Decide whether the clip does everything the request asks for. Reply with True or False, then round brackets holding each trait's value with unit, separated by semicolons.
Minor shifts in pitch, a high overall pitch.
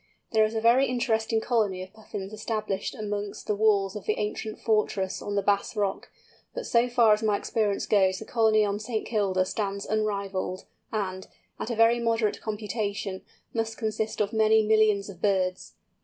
True (1.8 semitones; 215 Hz)